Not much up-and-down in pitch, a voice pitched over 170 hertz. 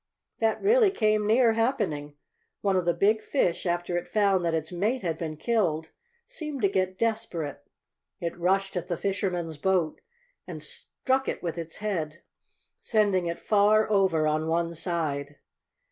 No: average, 4.4 semitones; medium, 185 Hz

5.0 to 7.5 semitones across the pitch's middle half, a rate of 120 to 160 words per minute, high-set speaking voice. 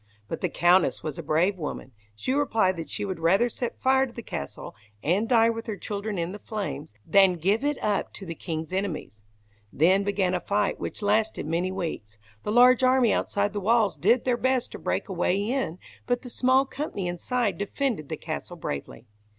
No: average, 5.3 semitones; average, 200 wpm; high, 200 Hz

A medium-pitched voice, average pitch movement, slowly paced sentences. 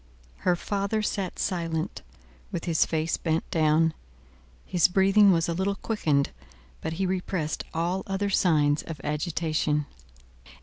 Yes: medium, 170 Hz; average, 3.3 semitones; slow, 130 wpm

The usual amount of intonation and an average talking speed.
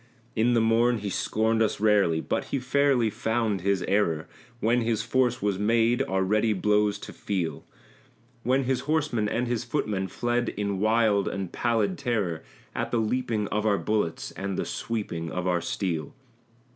Yes: average, 3.3 semitones; average, 170 wpm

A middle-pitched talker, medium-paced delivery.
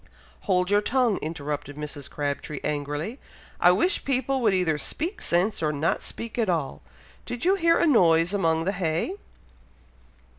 Yes: medium, 180 Hz; average, 155 wpm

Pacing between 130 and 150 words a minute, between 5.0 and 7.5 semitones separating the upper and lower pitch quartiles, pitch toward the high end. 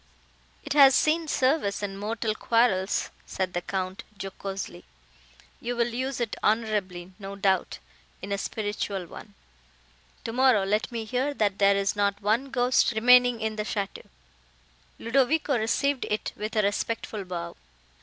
No: average, 145 wpm; average, 3.7 semitones; high, 215 Hz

